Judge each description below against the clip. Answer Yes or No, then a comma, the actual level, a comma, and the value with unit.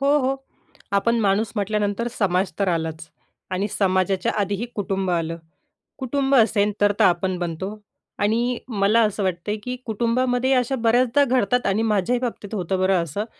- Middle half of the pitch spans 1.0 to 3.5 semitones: No, average, 4.1 semitones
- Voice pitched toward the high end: Yes, high, 205 Hz